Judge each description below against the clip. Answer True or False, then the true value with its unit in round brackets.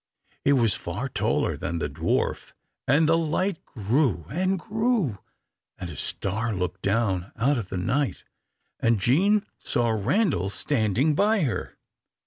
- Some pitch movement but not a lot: False (8.7 semitones)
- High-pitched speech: False (120 Hz)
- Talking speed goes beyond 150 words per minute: False (140 wpm)